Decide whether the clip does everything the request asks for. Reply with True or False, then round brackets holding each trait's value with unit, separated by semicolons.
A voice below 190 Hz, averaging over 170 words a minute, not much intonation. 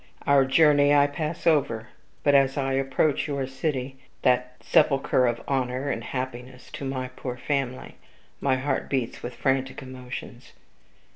False (135 Hz; 145 wpm; 1.9 semitones)